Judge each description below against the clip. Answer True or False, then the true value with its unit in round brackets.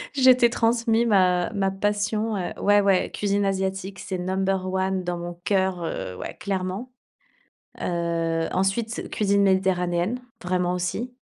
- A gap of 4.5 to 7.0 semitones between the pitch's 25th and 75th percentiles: False (2.4 semitones)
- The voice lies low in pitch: False (190 Hz)